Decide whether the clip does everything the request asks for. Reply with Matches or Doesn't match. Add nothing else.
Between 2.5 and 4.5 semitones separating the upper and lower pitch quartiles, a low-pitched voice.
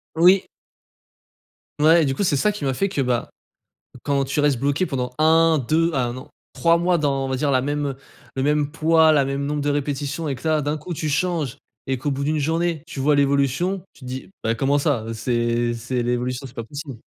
Doesn't match